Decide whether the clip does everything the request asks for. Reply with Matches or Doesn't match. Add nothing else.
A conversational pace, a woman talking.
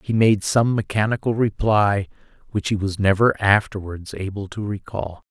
Doesn't match